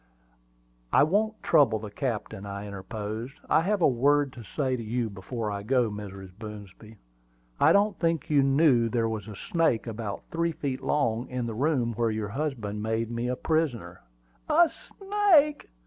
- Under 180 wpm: Yes, average, 170 wpm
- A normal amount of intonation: No, wide, 5.8 semitones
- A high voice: No, low, 120 Hz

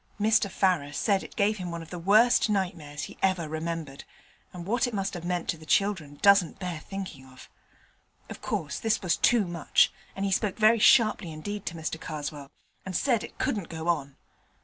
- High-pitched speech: No, medium, 180 Hz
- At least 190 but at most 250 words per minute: Yes, average, 195 wpm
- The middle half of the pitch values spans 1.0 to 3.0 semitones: No, average, 4.2 semitones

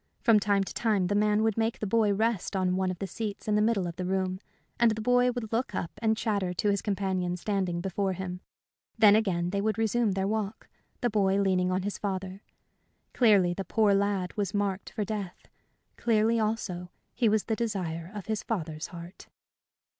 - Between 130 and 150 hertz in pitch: No, high, 200 Hz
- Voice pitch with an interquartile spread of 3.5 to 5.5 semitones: No, average, 2.7 semitones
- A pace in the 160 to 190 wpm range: No, average, 200 wpm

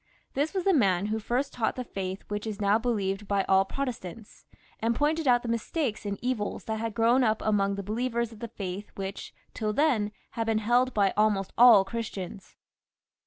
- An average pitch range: Yes, average, 3.3 semitones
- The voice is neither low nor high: No, high, 220 Hz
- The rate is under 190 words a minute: No, average, 195 wpm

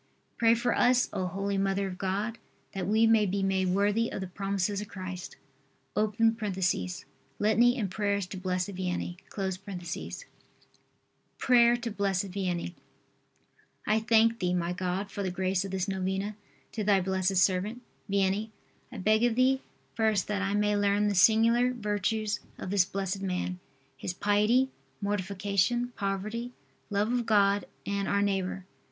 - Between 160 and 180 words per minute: No, average, 145 wpm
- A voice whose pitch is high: Yes, high, 200 Hz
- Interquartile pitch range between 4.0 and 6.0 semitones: No, narrow, 2.5 semitones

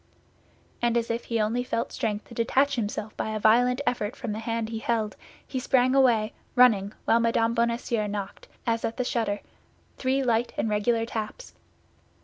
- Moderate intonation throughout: No, narrow, 2.1 semitones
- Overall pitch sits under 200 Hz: No, high, 230 Hz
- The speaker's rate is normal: Yes, average, 175 wpm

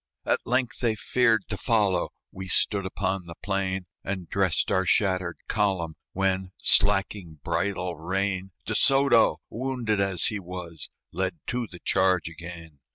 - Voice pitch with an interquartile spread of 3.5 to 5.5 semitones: No, narrow, 2.4 semitones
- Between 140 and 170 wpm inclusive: Yes, average, 145 wpm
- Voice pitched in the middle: No, very low, 95 Hz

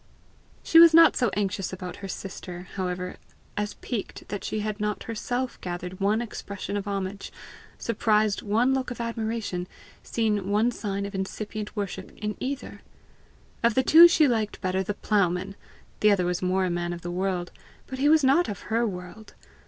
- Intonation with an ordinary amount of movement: Yes, average, 3.7 semitones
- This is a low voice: No, high, 205 Hz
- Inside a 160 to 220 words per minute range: Yes, average, 175 wpm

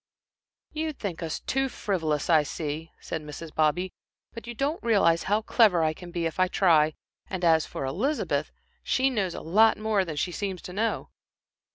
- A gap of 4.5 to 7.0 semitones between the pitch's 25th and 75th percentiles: Yes, average, 5.3 semitones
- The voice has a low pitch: No, medium, 180 Hz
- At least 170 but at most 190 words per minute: Yes, average, 185 wpm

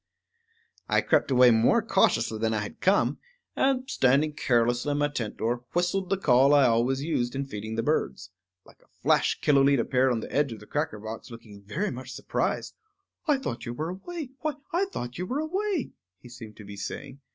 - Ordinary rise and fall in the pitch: No, wide, 7.7 semitones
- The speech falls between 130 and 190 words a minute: No, average, 200 wpm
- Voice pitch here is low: Yes, low, 130 Hz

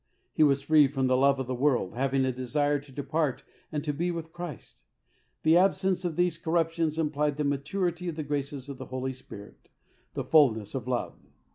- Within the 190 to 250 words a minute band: Yes, fast, 205 wpm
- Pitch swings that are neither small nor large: Yes, average, 3.5 semitones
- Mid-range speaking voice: Yes, medium, 145 Hz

